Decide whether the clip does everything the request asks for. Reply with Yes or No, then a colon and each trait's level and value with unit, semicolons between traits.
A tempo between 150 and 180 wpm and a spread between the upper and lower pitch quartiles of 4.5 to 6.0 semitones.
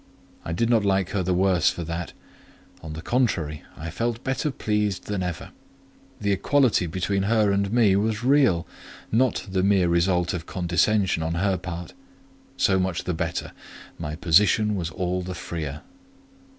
No: average, 160 wpm; average, 3.5 semitones